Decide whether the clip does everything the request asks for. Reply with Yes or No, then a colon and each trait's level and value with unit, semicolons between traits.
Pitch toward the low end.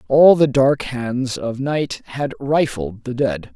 Yes: low, 130 Hz